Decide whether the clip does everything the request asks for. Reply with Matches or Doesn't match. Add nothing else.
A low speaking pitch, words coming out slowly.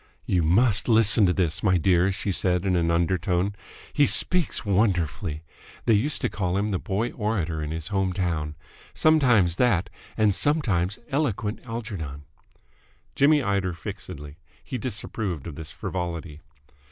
Doesn't match